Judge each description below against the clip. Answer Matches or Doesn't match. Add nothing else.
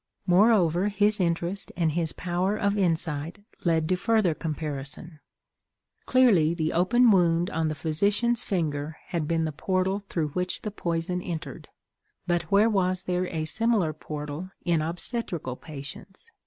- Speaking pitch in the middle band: Matches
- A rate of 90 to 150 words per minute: Matches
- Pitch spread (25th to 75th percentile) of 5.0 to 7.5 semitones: Doesn't match